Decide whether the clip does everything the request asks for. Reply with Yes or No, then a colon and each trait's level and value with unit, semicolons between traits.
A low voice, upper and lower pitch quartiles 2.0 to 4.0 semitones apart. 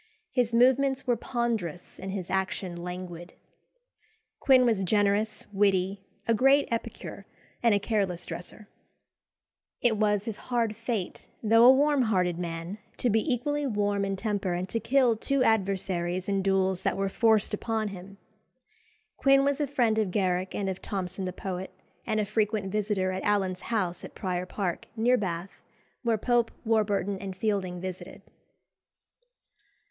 No: high, 205 Hz; average, 3.5 semitones